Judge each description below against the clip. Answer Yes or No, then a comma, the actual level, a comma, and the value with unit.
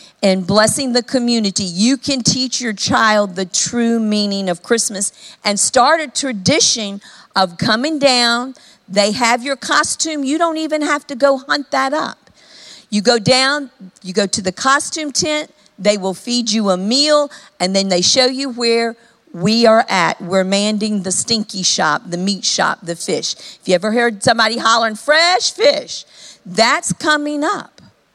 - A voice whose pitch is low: No, high, 230 Hz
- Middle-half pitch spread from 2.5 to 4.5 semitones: No, average, 5.2 semitones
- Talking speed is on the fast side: No, average, 170 wpm